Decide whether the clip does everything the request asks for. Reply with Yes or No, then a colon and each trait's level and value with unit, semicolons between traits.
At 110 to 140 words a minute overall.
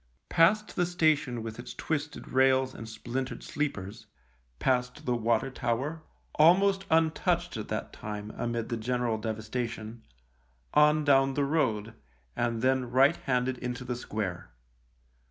Yes: slow, 135 wpm